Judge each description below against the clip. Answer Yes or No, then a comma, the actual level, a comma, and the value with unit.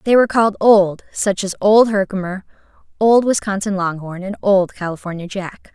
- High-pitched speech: Yes, high, 195 Hz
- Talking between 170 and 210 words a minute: No, average, 155 wpm